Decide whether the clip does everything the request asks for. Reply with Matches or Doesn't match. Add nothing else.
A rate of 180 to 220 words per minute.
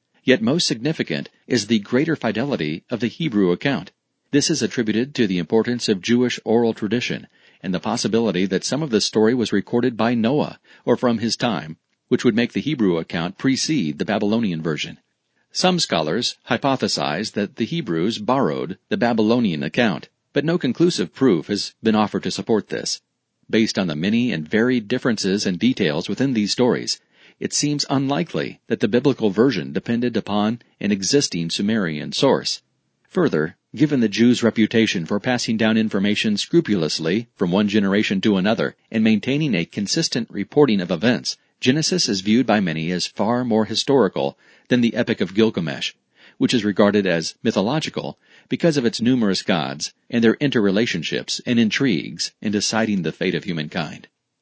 Doesn't match